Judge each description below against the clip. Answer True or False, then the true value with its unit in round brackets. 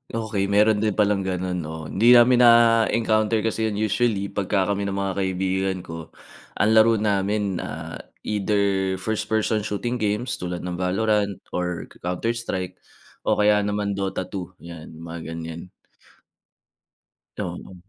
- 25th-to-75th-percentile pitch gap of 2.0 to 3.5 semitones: True (2.8 semitones)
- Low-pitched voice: True (100 Hz)